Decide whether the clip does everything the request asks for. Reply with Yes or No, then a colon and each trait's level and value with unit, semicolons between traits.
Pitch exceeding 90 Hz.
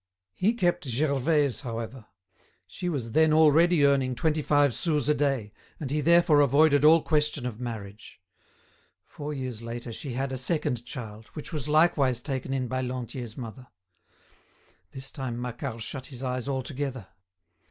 Yes: low, 135 Hz